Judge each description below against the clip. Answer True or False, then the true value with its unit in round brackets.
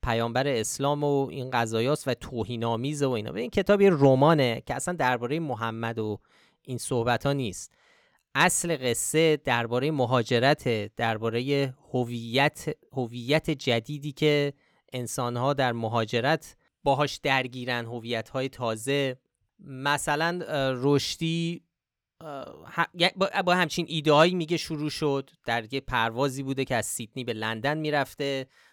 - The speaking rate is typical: True (120 wpm)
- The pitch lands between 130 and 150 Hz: True (135 Hz)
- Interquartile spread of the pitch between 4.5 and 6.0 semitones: False (3.9 semitones)